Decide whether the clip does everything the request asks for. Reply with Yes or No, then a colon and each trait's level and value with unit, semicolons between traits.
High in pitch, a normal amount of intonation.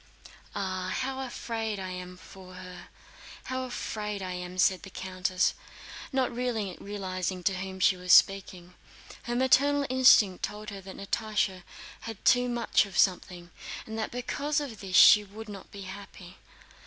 Yes: high, 200 Hz; average, 3.9 semitones